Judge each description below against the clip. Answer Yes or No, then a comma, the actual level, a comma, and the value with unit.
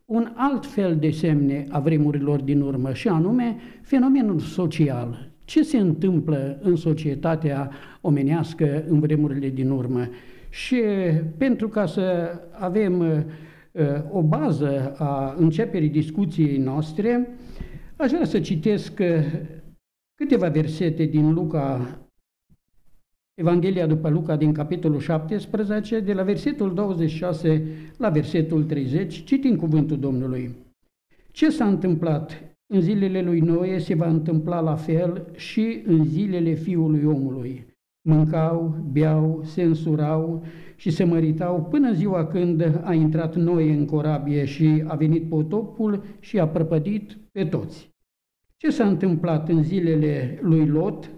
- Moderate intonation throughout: Yes, average, 3.5 semitones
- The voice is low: No, medium, 165 Hz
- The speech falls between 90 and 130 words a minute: Yes, average, 125 wpm